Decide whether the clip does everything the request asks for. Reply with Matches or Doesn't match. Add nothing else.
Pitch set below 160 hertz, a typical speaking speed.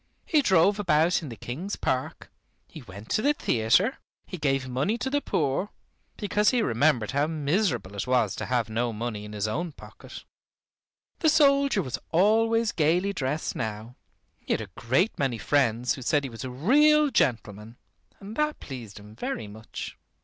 Matches